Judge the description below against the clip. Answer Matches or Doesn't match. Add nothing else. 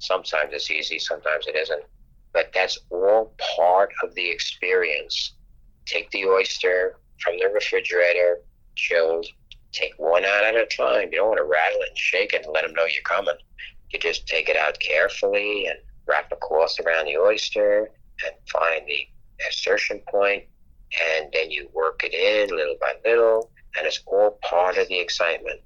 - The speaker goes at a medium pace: Matches